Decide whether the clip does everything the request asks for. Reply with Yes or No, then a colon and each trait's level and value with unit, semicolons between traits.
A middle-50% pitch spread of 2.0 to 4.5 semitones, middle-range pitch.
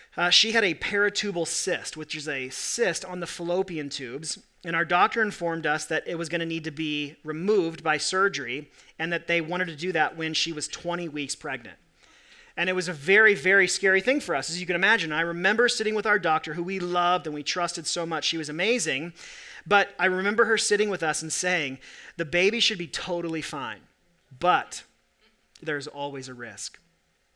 Yes: average, 3.3 semitones; medium, 170 Hz